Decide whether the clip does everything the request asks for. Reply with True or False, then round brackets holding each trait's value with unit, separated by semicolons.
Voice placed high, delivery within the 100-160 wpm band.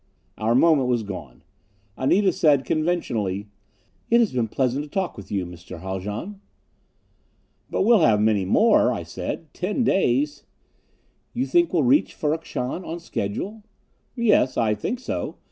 False (140 Hz; 150 wpm)